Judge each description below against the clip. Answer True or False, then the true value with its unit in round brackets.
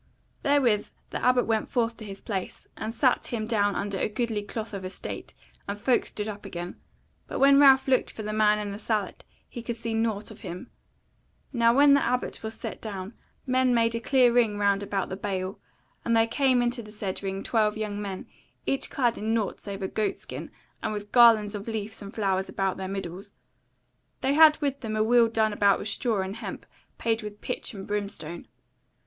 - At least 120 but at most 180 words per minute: False (205 wpm)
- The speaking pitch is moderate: False (215 Hz)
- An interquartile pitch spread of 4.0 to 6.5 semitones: False (2.7 semitones)